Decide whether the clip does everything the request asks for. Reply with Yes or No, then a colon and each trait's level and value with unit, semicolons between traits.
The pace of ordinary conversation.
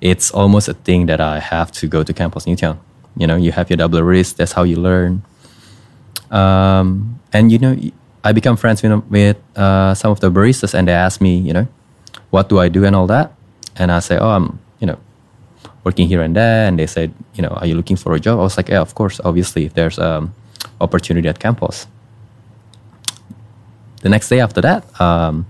No: fast, 215 wpm